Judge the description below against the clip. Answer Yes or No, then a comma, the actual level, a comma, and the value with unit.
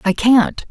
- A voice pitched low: No, high, 205 Hz